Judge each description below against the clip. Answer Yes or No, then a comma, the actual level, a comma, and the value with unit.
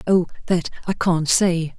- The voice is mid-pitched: Yes, medium, 175 Hz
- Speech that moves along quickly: No, average, 170 wpm